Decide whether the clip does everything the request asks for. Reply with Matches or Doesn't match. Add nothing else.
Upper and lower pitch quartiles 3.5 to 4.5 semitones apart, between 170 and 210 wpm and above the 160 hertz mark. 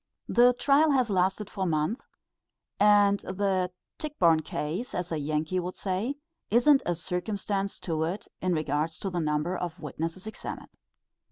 Doesn't match